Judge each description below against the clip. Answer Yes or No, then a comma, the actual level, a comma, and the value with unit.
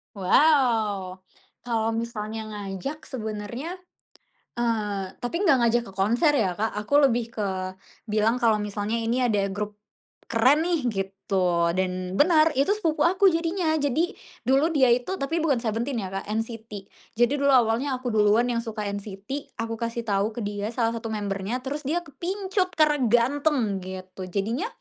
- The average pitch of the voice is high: Yes, high, 230 Hz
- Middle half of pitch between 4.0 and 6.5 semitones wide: Yes, average, 5.2 semitones